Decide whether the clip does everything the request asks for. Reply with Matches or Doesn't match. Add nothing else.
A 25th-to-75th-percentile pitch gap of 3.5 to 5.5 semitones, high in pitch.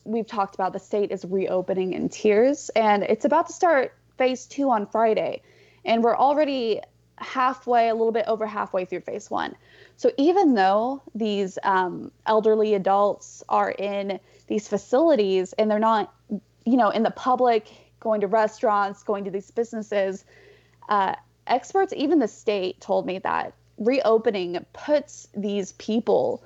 Matches